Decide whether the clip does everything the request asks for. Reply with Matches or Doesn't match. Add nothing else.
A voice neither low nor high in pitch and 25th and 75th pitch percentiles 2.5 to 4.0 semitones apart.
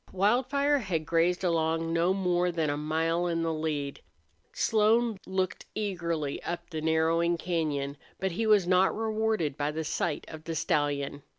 Matches